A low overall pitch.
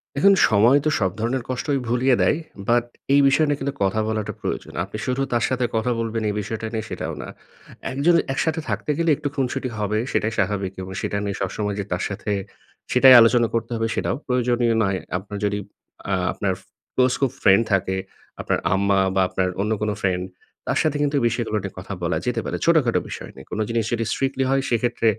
Yes: low, 115 Hz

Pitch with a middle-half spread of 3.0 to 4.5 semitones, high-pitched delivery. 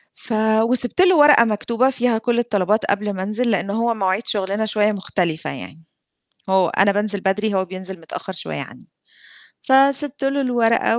Yes: average, 4.0 semitones; high, 215 Hz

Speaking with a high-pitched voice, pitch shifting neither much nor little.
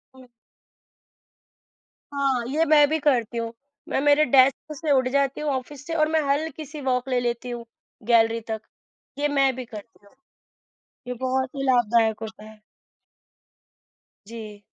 Yes: very high, 260 Hz; average, 3.7 semitones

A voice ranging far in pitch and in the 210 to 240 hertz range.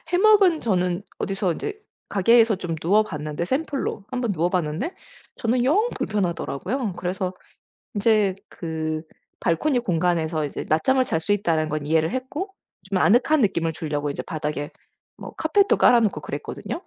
No: wide, 7.6 semitones; high, 190 Hz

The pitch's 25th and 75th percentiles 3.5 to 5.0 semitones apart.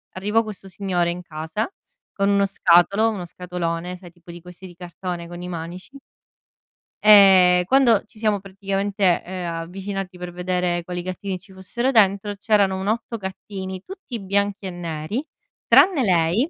No: narrow, 2.4 semitones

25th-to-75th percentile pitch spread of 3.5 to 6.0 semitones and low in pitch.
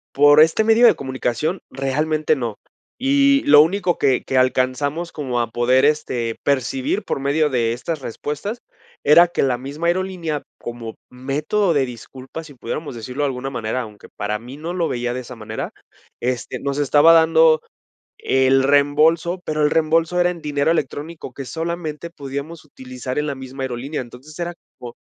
No: average, 4.2 semitones; medium, 145 Hz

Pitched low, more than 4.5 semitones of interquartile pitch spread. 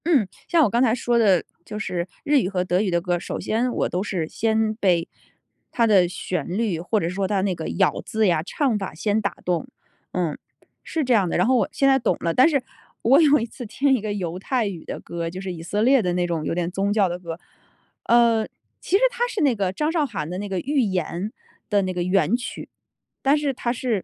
No: high, 205 Hz; average, 5.3 semitones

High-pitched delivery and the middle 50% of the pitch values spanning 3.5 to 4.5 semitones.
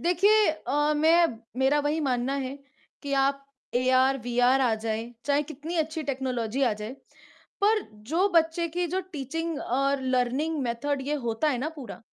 Yes: very high, 275 Hz; average, 4.0 semitones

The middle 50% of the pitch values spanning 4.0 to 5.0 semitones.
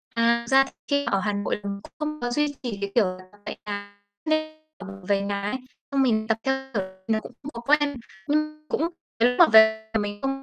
No: wide, 5.4 semitones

